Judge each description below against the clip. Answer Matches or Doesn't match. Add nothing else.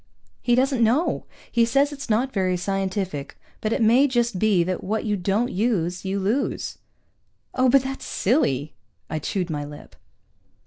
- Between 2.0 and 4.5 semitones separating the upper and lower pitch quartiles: Doesn't match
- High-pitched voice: Matches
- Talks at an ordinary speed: Matches